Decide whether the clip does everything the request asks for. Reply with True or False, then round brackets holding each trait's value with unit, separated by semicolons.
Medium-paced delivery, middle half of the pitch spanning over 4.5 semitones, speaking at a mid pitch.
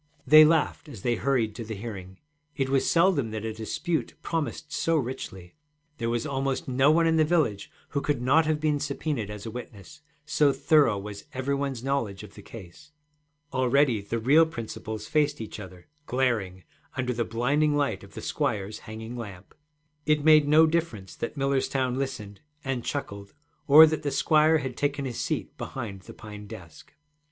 False (180 wpm; 5.3 semitones; 130 Hz)